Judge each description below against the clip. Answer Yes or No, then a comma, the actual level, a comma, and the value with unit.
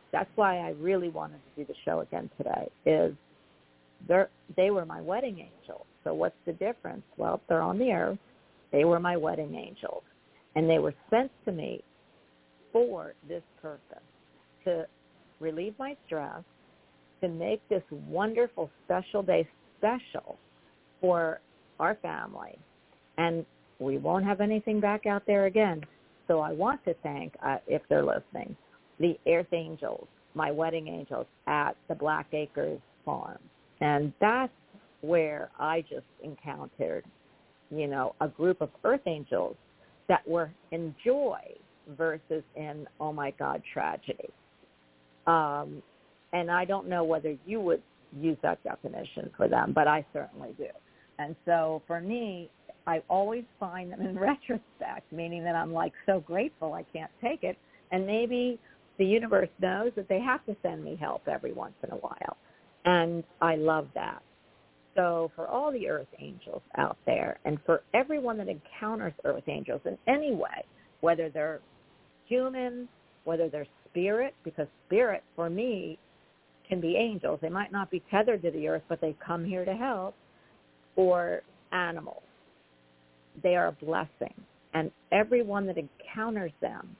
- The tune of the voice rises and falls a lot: No, average, 4.5 semitones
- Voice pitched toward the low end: No, medium, 170 Hz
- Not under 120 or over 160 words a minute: Yes, average, 155 wpm